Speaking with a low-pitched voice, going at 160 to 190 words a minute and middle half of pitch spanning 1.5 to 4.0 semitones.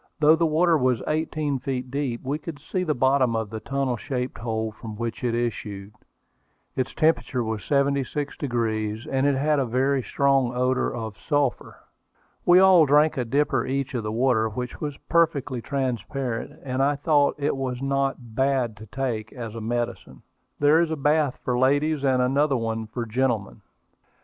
Yes: low, 130 Hz; average, 175 wpm; average, 3.4 semitones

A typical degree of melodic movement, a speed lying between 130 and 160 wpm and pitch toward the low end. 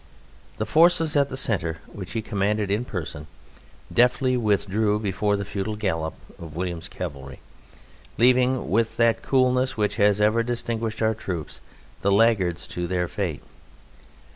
Yes: average, 4.0 semitones; average, 140 wpm; low, 105 Hz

